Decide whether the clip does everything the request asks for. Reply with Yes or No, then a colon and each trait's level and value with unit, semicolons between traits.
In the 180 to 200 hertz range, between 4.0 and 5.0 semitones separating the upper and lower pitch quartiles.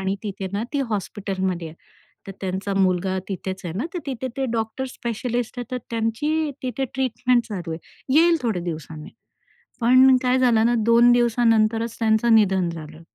No: high, 225 Hz; average, 4.4 semitones